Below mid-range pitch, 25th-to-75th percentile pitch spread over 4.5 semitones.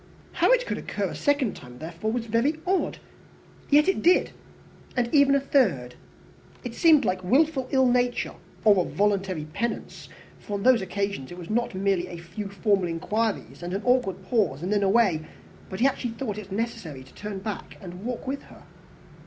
No: high, 210 Hz; average, 5.3 semitones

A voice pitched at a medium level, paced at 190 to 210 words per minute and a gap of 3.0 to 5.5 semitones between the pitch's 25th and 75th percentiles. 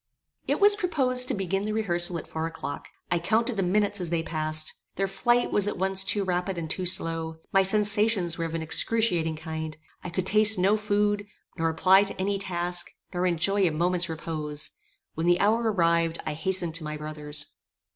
Yes: medium, 180 Hz; average, 195 wpm; average, 3.9 semitones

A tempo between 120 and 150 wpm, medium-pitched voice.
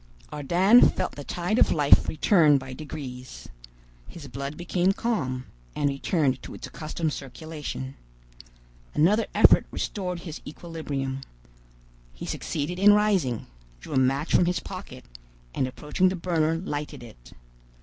Yes: slow, 135 wpm; medium, 155 Hz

